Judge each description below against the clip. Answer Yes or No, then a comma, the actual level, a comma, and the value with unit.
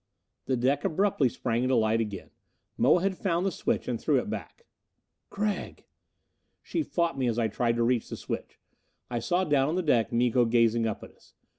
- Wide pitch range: Yes, wide, 6.6 semitones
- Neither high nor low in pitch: No, low, 125 Hz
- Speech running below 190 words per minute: No, average, 195 wpm